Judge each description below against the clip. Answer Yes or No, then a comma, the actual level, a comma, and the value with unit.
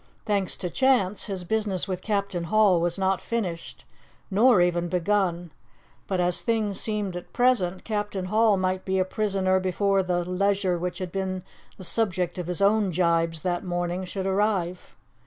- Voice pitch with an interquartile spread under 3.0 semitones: Yes, narrow, 2.4 semitones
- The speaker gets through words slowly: No, average, 165 wpm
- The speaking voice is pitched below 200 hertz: Yes, high, 190 Hz